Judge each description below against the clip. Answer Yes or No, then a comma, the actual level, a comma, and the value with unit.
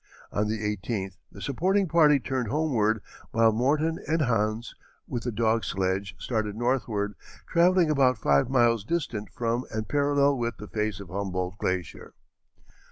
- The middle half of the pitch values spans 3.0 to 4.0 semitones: No, average, 5.0 semitones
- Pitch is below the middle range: Yes, low, 115 Hz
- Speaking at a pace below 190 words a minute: Yes, average, 150 wpm